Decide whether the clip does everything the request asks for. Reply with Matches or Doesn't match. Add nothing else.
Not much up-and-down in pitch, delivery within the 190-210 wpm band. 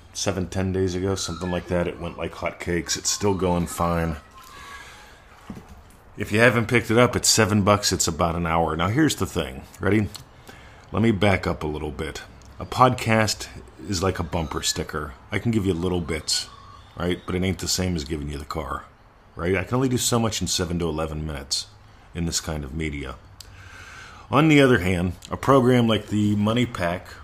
Doesn't match